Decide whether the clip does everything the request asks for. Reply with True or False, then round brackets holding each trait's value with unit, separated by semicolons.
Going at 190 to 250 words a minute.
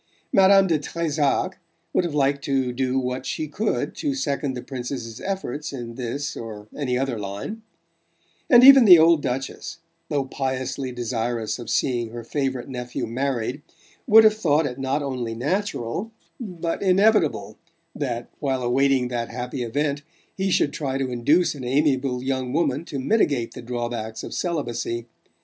False (155 wpm)